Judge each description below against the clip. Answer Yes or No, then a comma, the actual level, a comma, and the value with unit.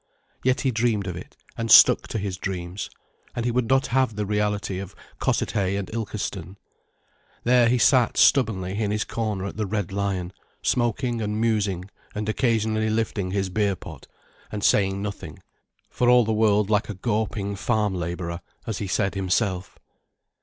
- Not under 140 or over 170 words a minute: Yes, average, 165 wpm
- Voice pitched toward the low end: Yes, low, 105 Hz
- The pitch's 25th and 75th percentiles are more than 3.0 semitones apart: No, average, 2.7 semitones